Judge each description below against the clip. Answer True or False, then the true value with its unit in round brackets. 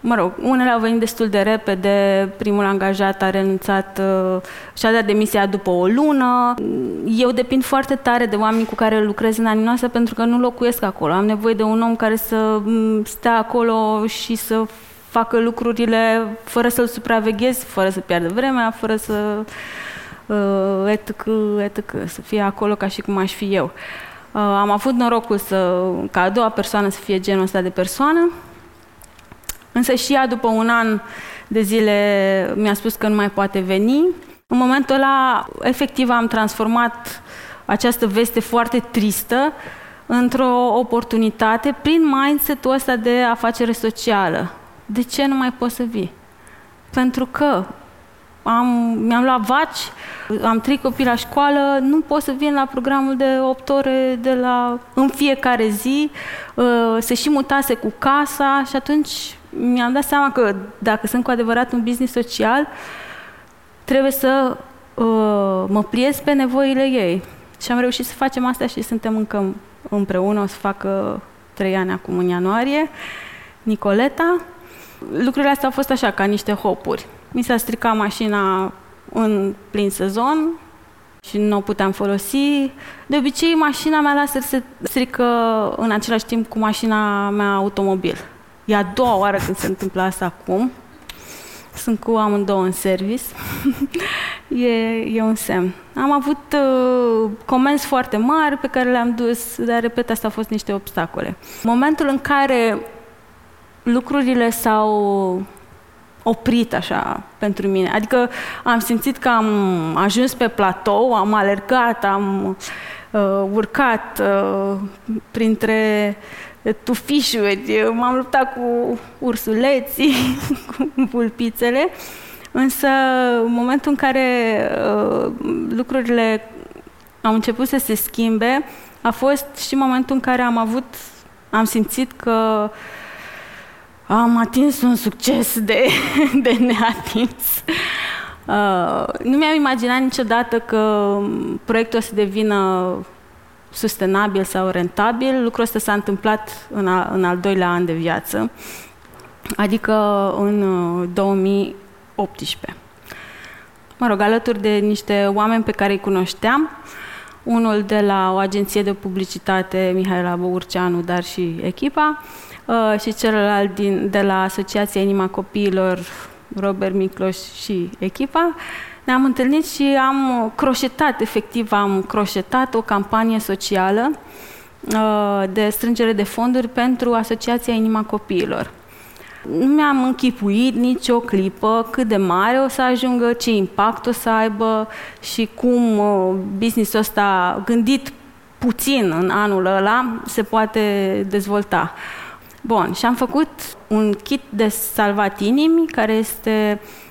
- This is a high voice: True (225 Hz)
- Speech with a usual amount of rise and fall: True (3.9 semitones)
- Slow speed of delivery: False (135 wpm)